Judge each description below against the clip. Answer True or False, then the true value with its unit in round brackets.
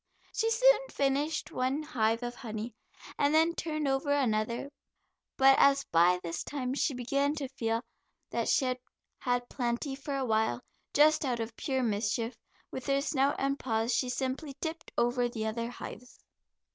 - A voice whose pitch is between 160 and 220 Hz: False (260 Hz)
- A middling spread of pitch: True (3.4 semitones)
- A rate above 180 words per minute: False (165 wpm)